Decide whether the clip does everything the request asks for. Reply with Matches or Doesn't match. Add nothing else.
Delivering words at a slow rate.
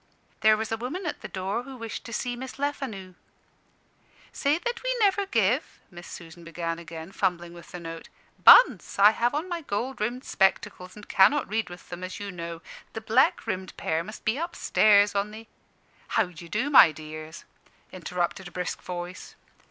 Doesn't match